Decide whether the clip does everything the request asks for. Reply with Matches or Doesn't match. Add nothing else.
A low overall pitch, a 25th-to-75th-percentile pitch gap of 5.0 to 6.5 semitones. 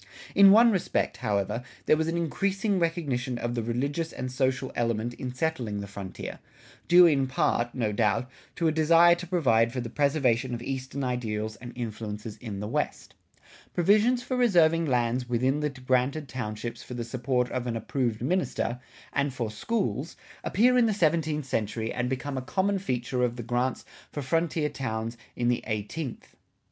Matches